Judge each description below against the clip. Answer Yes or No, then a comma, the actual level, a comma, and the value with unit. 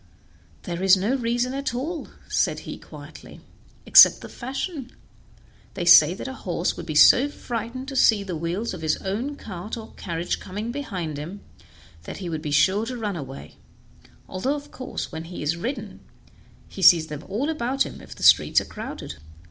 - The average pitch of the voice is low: No, high, 205 Hz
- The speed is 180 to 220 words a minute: Yes, average, 185 wpm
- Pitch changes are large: Yes, wide, 6.9 semitones